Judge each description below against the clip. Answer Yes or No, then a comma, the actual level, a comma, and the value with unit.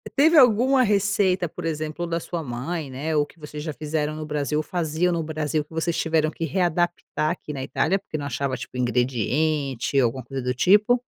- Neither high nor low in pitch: Yes, medium, 155 Hz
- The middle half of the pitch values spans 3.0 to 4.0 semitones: Yes, average, 3.5 semitones